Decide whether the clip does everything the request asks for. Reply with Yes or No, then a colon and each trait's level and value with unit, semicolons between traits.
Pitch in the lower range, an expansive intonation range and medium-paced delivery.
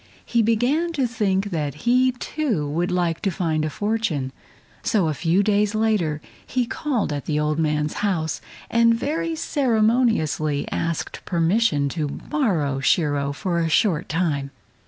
No: medium, 180 Hz; wide, 7.0 semitones; average, 150 wpm